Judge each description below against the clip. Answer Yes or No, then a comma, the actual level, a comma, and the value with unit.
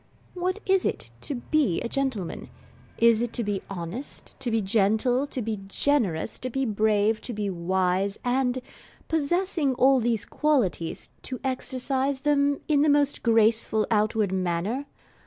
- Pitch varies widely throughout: No, average, 4.9 semitones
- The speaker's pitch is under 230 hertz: No, high, 240 Hz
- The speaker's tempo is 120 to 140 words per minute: No, average, 150 wpm